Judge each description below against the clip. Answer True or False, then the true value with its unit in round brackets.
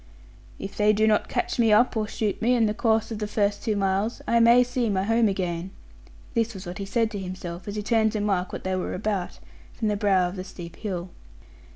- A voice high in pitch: True (210 Hz)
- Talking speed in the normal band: False (240 wpm)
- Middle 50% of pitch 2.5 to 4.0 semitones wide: True (2.9 semitones)